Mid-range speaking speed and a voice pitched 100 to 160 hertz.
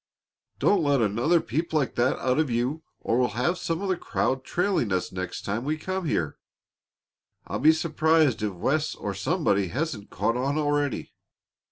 Yes: average, 175 wpm; medium, 140 Hz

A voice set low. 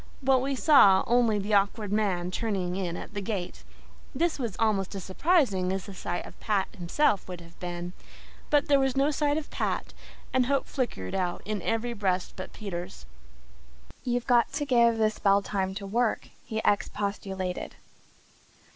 No: high, 205 Hz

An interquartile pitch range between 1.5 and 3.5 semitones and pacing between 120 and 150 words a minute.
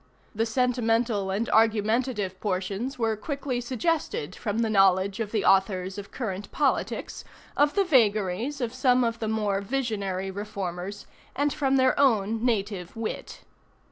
No: average, 4.2 semitones; average, 140 wpm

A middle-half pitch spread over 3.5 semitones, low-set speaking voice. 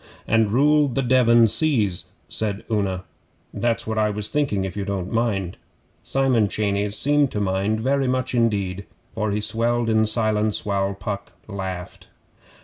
No: average, 3.1 semitones; low, 110 Hz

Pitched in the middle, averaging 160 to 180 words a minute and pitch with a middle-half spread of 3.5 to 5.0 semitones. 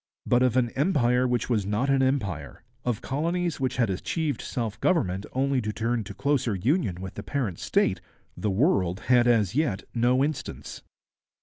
No: low, 125 Hz; average, 175 wpm; average, 4.7 semitones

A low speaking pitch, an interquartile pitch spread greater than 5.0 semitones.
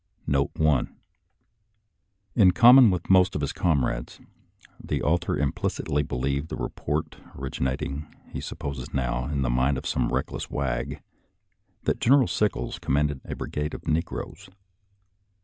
Yes: very low, 75 Hz; wide, 5.5 semitones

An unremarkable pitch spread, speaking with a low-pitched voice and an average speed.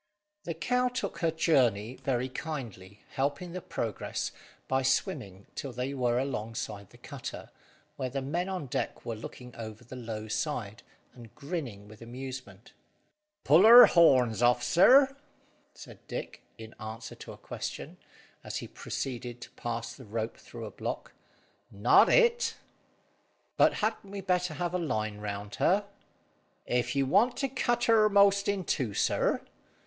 No: wide, 7.9 semitones; low, 130 Hz; average, 155 wpm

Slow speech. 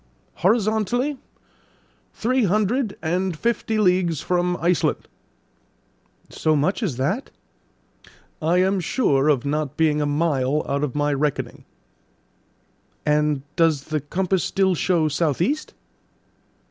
Yes: slow, 115 wpm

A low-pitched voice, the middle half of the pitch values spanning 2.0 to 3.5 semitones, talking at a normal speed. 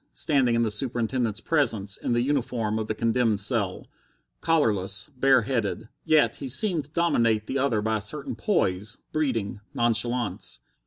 No: low, 115 Hz; average, 4.1 semitones; average, 155 wpm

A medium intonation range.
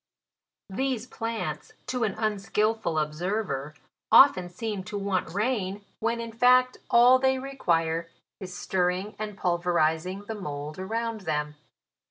Yes: average, 4.7 semitones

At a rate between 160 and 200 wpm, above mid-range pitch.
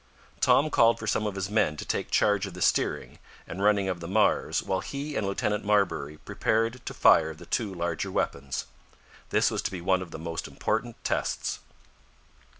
No: average, 190 wpm; low, 100 Hz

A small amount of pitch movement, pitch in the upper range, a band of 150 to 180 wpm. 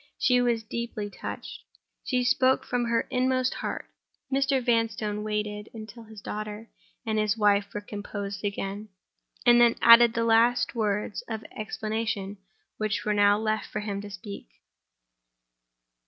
No: narrow, 2.2 semitones; high, 215 Hz; average, 140 wpm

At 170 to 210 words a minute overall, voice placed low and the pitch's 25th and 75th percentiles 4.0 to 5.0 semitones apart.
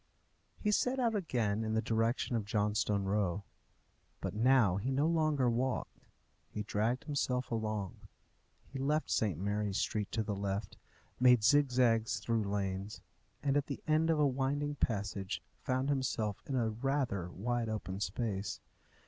No: average, 150 wpm; low, 115 Hz; average, 4.6 semitones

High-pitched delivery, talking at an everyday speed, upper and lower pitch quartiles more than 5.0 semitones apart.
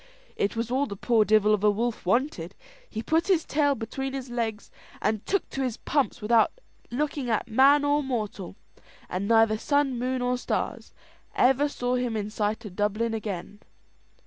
No: high, 235 Hz; average, 175 wpm; average, 4.0 semitones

